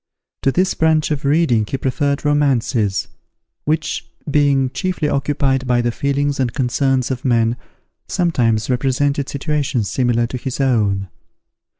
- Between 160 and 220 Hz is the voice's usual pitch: No, low, 135 Hz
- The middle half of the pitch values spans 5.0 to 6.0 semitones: No, average, 3.1 semitones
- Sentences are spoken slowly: Yes, slow, 130 wpm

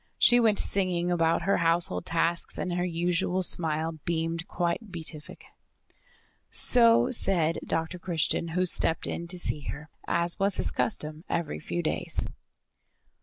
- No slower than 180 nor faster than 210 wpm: No, average, 140 wpm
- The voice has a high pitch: No, medium, 170 Hz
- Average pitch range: No, narrow, 1.9 semitones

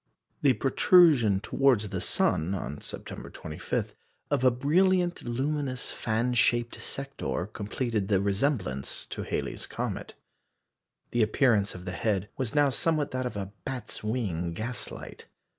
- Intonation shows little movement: No, average, 5.3 semitones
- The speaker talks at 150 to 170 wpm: No, slow, 135 wpm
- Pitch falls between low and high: No, low, 120 Hz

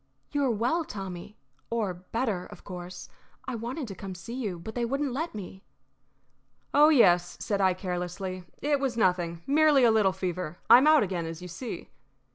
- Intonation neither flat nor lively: No, wide, 6.1 semitones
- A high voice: Yes, high, 200 Hz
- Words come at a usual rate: Yes, average, 190 wpm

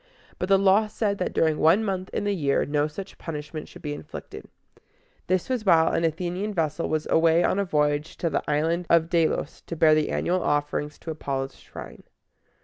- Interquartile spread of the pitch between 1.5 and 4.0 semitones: Yes, average, 3.6 semitones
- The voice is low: No, medium, 165 Hz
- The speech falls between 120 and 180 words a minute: No, average, 195 wpm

